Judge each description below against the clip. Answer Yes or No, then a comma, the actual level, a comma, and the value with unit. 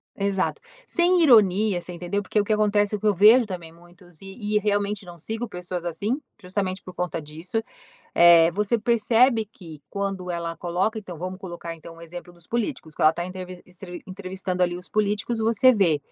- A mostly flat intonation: No, average, 3.2 semitones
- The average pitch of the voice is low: No, medium, 185 Hz